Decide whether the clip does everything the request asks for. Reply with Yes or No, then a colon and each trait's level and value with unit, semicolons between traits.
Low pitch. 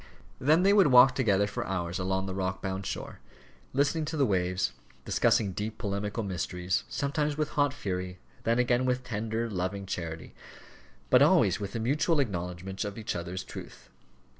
Yes: low, 105 Hz